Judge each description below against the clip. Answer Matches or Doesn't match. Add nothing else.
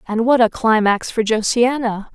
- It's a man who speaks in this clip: Doesn't match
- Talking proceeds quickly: Doesn't match